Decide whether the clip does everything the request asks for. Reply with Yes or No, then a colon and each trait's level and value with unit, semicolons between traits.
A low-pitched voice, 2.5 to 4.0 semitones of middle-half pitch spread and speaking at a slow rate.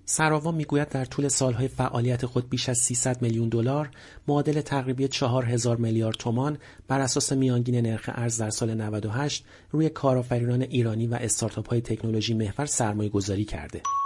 No: low, 125 Hz; average, 3.2 semitones; fast, 155 wpm